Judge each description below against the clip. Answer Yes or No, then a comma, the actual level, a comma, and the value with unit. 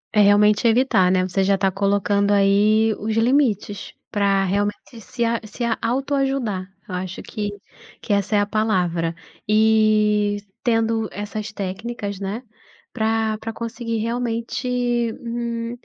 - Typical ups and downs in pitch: No, narrow, 2.3 semitones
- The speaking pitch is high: Yes, high, 215 Hz